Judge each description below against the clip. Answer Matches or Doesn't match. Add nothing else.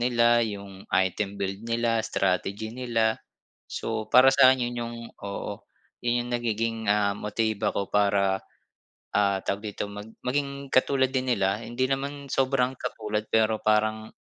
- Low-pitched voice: Matches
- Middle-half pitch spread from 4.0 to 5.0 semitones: Doesn't match